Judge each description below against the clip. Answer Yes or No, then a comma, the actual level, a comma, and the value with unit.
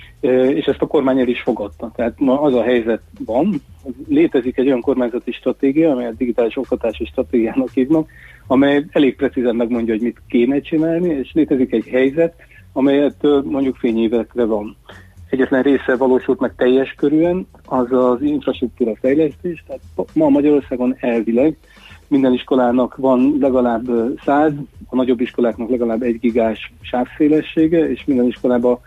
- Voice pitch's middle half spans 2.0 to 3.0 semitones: Yes, average, 2.7 semitones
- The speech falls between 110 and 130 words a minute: No, average, 140 wpm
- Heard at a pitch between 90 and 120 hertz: No, low, 130 Hz